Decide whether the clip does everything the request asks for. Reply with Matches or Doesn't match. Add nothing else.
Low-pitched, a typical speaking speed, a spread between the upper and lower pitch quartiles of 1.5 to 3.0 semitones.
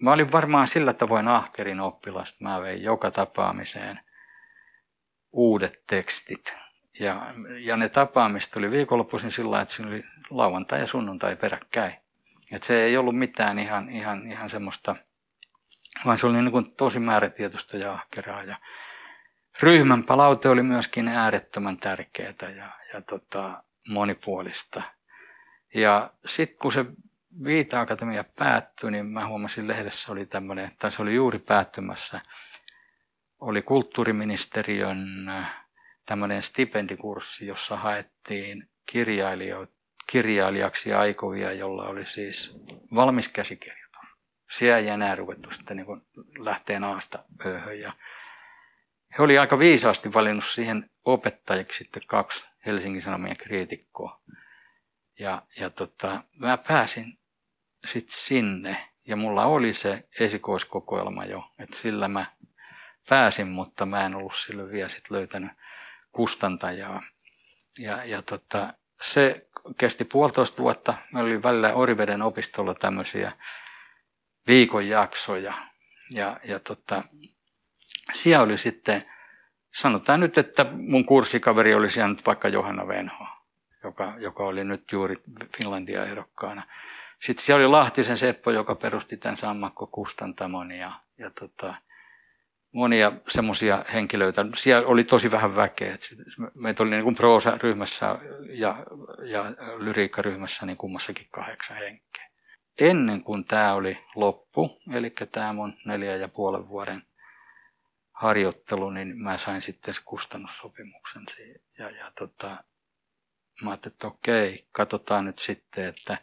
Doesn't match